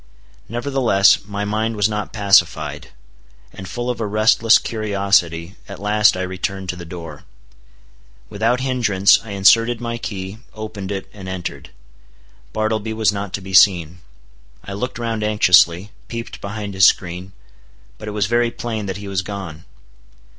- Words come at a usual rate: Yes, average, 155 wpm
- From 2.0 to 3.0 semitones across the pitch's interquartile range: Yes, average, 2.7 semitones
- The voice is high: No, low, 100 Hz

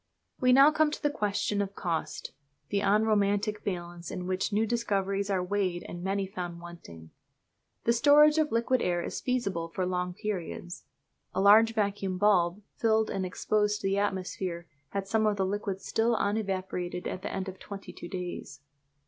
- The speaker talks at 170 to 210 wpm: Yes, average, 175 wpm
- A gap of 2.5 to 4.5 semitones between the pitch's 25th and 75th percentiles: Yes, average, 2.9 semitones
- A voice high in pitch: Yes, high, 200 Hz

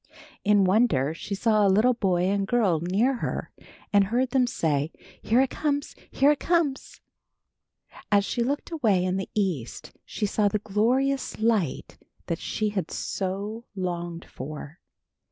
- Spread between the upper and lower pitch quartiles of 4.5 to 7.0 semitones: Yes, average, 4.8 semitones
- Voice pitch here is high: Yes, high, 205 Hz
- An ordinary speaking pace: Yes, average, 155 wpm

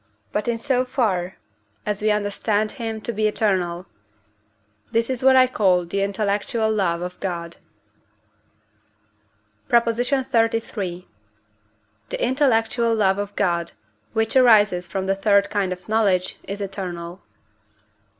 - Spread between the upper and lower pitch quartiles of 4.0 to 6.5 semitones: No, average, 3.4 semitones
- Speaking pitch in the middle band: No, high, 210 Hz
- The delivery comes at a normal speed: No, slow, 125 wpm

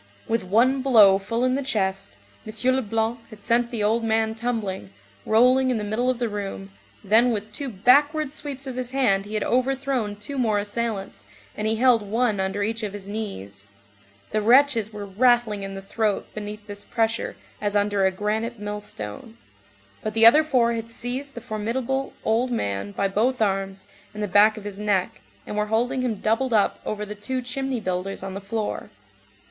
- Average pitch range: Yes, average, 3.3 semitones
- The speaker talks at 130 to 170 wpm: No, average, 190 wpm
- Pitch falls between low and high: No, high, 220 Hz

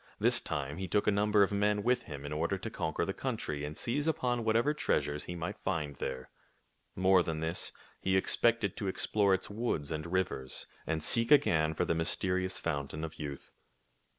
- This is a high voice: No, very low, 95 Hz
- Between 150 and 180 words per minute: No, average, 190 wpm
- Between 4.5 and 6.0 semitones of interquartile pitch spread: Yes, average, 5.2 semitones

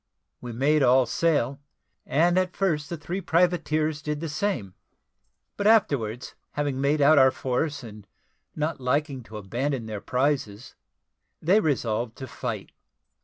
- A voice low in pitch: No, medium, 145 Hz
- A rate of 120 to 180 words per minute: Yes, average, 140 wpm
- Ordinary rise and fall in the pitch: Yes, average, 4.1 semitones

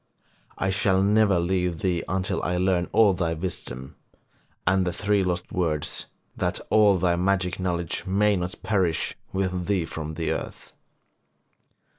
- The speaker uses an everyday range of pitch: No, narrow, 2.0 semitones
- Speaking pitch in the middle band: No, very low, 90 Hz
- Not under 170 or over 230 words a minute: No, average, 145 wpm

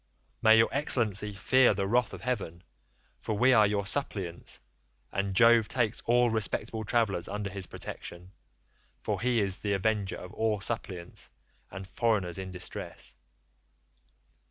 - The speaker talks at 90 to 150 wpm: Yes, average, 140 wpm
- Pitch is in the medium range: No, low, 105 Hz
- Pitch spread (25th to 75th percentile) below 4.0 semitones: Yes, average, 3.1 semitones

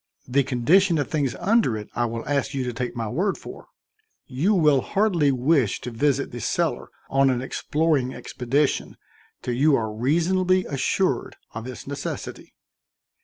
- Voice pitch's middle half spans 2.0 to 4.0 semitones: No, average, 4.7 semitones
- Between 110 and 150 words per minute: No, average, 160 wpm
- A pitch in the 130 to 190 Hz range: Yes, low, 135 Hz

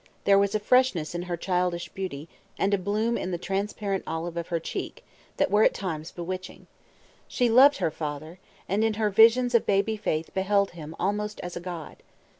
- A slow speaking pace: No, average, 195 wpm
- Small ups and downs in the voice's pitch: No, average, 3.5 semitones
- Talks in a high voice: Yes, high, 195 Hz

